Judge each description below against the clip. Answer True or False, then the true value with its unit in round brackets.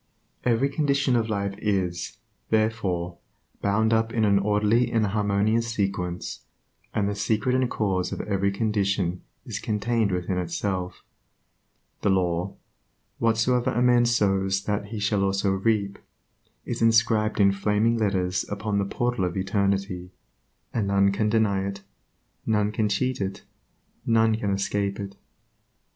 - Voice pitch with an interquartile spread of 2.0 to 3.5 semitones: True (2.4 semitones)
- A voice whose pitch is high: False (100 Hz)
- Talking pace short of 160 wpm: True (140 wpm)